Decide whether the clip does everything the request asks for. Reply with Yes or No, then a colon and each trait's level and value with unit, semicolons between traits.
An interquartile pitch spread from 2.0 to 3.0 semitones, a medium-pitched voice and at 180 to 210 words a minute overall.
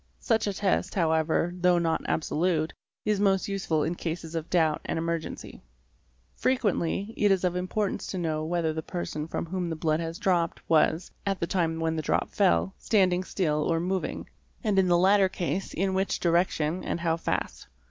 Yes: average, 2.7 semitones; medium, 175 Hz; average, 190 wpm